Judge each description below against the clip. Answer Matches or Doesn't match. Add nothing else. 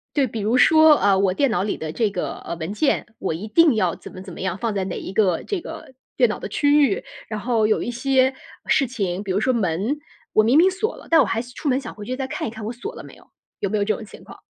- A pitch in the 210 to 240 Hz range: Matches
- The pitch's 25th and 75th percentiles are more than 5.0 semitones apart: Matches